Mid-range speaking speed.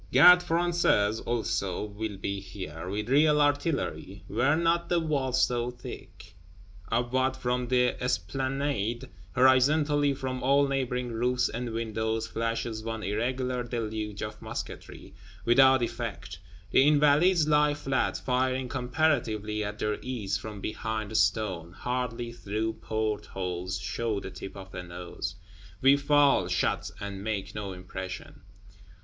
No: slow, 130 wpm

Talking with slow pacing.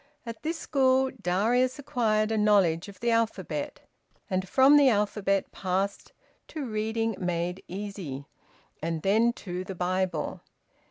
Yes: slow, 130 wpm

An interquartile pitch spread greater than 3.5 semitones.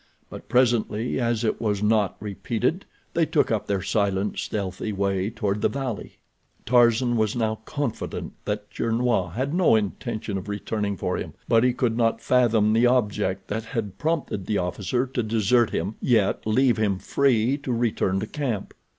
No: average, 3.1 semitones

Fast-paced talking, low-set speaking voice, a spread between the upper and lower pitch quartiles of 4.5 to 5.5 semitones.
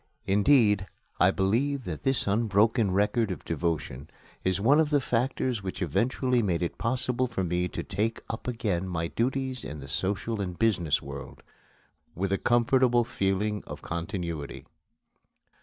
No: average, 150 wpm; low, 105 Hz; average, 4.8 semitones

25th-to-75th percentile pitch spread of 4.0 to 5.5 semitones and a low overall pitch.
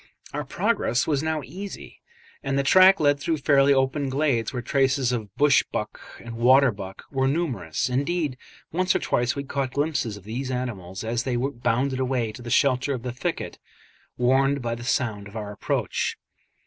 No: average, 3.1 semitones; low, 130 Hz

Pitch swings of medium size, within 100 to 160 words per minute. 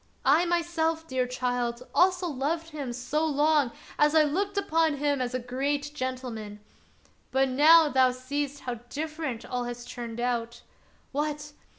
Yes: average, 3.9 semitones; average, 150 wpm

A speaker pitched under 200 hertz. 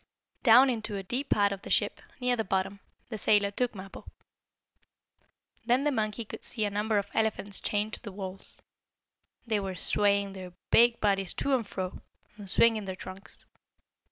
No: high, 205 Hz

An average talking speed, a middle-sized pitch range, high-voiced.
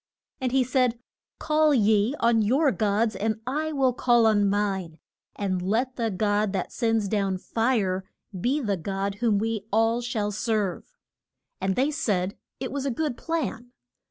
Yes: average, 160 wpm; average, 4.0 semitones; high, 225 Hz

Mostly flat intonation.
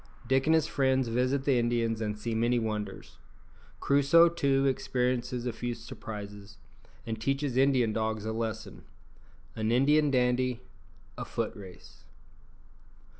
No: average, 3.4 semitones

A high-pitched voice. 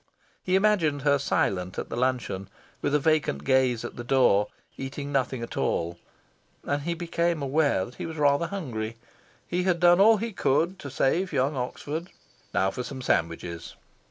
No: medium, 140 Hz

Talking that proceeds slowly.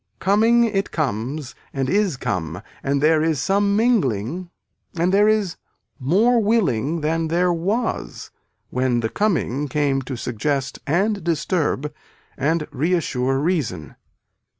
Yes: slow, 125 wpm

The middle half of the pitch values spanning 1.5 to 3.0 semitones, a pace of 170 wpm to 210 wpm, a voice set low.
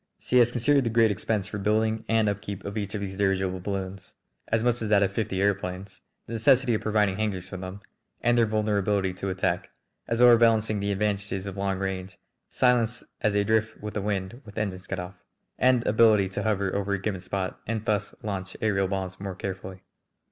Yes: narrow, 2.4 semitones; average, 200 wpm; low, 100 Hz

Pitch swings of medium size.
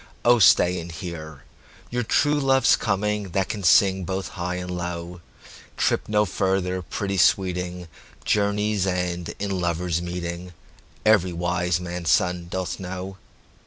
No: narrow, 2.0 semitones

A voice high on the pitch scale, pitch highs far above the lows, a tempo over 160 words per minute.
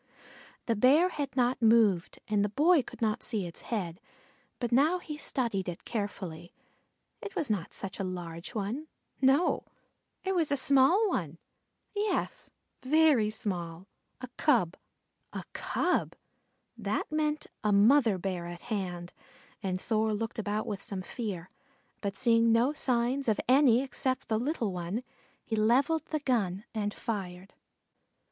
No: high, 225 Hz; wide, 5.8 semitones; average, 145 wpm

